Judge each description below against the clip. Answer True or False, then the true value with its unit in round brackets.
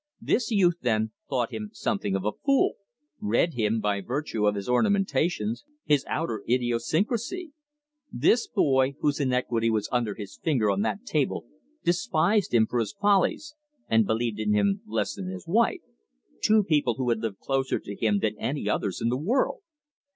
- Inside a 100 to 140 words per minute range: False (170 wpm)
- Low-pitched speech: True (125 Hz)